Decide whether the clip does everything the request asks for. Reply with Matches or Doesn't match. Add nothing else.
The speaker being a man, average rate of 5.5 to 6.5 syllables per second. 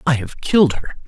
Matches